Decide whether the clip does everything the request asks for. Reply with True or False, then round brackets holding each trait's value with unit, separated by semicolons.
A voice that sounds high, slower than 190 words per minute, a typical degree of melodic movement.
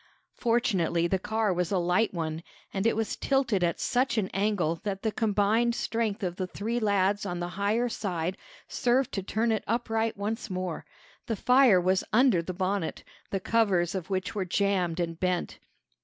True (200 Hz; 180 wpm; 3.7 semitones)